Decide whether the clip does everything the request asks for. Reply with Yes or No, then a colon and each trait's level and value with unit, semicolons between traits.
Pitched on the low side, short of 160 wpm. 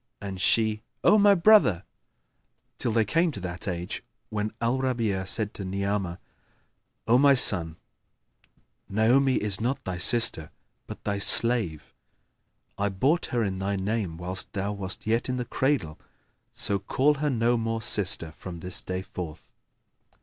Yes: low, 105 Hz; average, 150 wpm